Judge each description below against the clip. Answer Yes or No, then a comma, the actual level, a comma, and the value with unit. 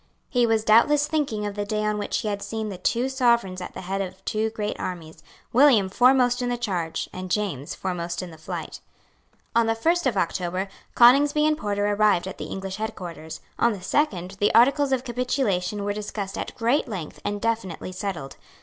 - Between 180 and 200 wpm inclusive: Yes, average, 195 wpm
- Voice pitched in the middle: No, high, 210 Hz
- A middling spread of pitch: Yes, average, 4.3 semitones